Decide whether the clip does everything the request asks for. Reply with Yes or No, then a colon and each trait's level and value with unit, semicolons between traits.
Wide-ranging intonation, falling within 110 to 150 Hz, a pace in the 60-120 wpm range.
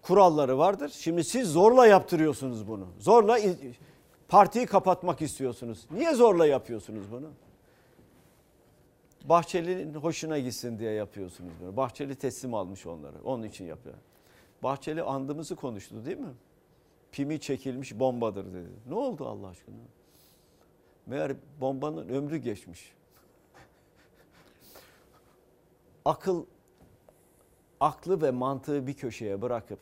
Yes: wide, 6.7 semitones; low, 135 Hz; average, 105 wpm